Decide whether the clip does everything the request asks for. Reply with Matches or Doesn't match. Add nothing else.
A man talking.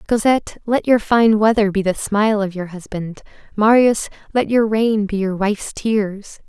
Doesn't match